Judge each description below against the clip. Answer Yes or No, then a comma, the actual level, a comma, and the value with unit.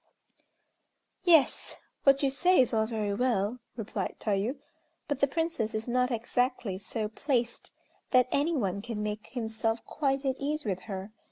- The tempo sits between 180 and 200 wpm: No, average, 155 wpm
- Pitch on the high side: Yes, high, 240 Hz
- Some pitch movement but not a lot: Yes, average, 4.1 semitones